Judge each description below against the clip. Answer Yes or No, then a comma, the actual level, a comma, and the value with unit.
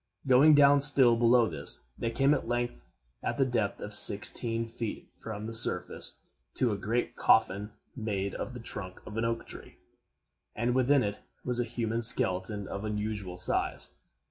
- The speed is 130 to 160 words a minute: No, average, 170 wpm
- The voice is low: Yes, low, 115 Hz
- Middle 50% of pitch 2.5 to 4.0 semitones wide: Yes, average, 2.9 semitones